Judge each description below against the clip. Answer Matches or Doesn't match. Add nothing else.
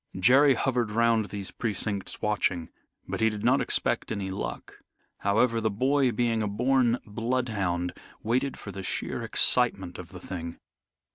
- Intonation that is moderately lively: Matches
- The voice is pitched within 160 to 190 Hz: Doesn't match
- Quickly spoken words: Doesn't match